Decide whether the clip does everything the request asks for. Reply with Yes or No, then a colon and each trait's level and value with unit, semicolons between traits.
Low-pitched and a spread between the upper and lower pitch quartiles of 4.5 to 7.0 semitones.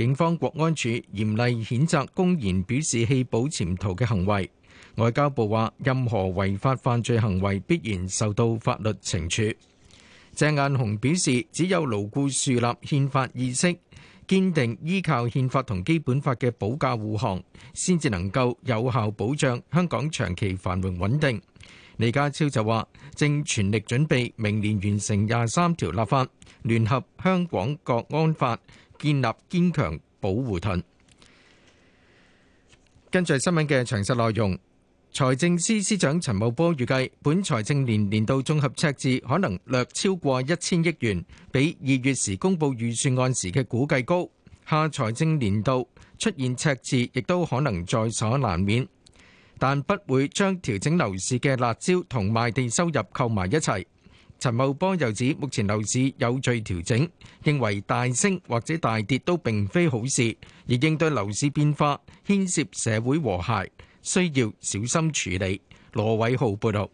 Yes: low, 125 Hz; wide, 5.5 semitones